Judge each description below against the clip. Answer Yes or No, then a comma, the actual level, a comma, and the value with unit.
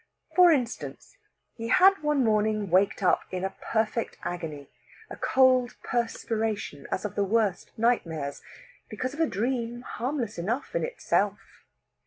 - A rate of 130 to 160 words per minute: Yes, average, 140 wpm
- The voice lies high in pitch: Yes, high, 225 Hz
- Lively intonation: No, average, 4.5 semitones